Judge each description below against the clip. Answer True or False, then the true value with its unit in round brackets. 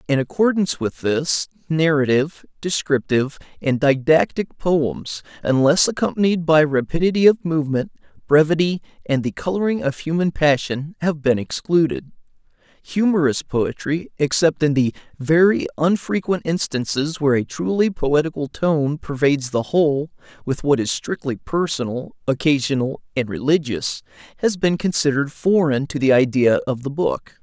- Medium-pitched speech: True (150 Hz)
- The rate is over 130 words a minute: False (125 wpm)